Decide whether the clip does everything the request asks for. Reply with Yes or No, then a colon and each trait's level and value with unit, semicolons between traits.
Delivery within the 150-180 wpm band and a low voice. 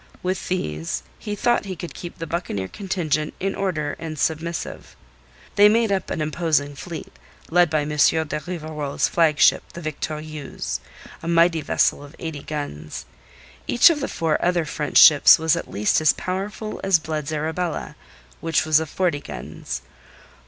No: average, 160 wpm; medium, 160 Hz